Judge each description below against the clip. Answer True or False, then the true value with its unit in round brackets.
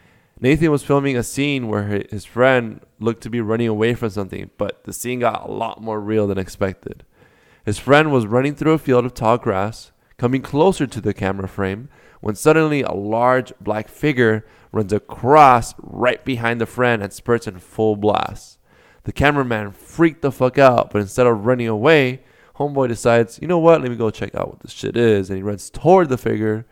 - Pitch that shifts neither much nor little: True (3.9 semitones)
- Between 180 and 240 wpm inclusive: True (200 wpm)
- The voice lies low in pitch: True (115 Hz)